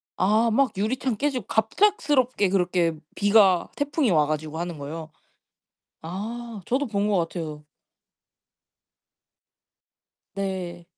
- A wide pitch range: Yes, wide, 5.8 semitones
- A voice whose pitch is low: No, high, 200 Hz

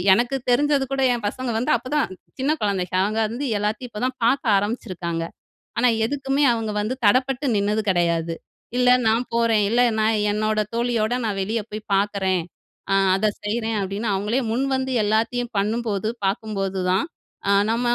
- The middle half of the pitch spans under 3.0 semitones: No, average, 3.3 semitones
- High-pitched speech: Yes, high, 220 Hz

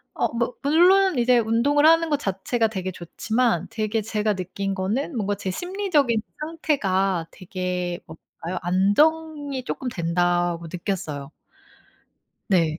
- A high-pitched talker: Yes, high, 215 Hz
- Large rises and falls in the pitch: Yes, wide, 7.6 semitones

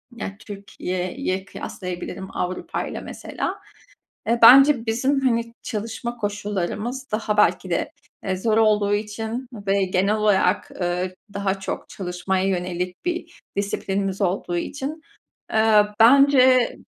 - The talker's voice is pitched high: Yes, high, 205 Hz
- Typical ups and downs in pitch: Yes, average, 3.6 semitones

